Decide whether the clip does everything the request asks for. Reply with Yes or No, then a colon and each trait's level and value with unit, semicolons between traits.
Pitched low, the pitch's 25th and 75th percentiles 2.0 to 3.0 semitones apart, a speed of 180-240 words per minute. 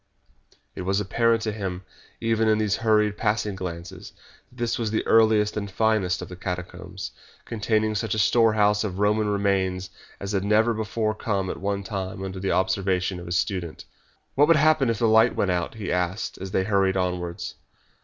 Yes: low, 100 Hz; average, 2.7 semitones; average, 185 wpm